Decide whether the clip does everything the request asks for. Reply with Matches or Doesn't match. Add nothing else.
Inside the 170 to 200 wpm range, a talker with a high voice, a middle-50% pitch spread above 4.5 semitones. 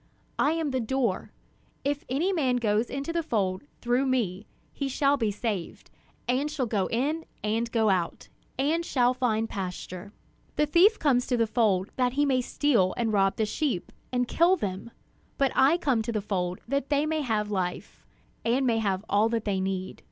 Matches